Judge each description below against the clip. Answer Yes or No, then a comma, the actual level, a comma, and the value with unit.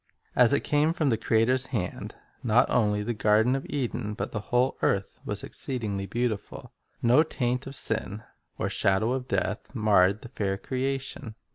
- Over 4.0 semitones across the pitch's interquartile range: No, average, 3.7 semitones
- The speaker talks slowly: No, average, 165 wpm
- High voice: No, low, 120 Hz